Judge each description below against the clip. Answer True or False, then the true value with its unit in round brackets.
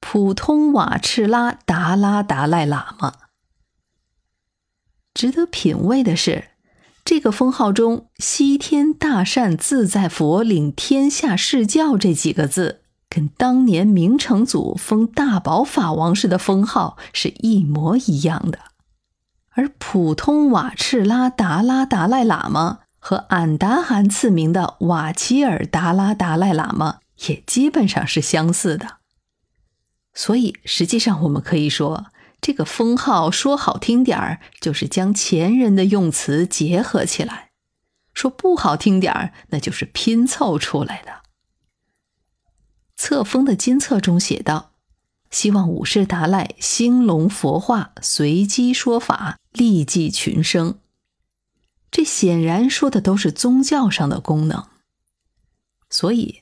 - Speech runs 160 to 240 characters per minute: True (190 characters per minute)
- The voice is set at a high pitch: True (200 Hz)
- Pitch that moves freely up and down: True (6.9 semitones)